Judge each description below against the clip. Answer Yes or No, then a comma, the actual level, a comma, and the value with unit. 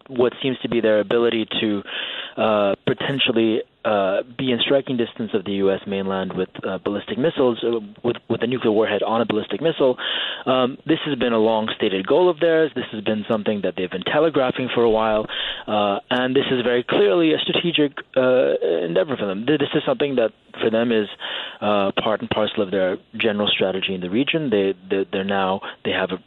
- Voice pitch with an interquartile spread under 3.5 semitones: No, average, 4.0 semitones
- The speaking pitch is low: Yes, low, 115 Hz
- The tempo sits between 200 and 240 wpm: Yes, fast, 205 wpm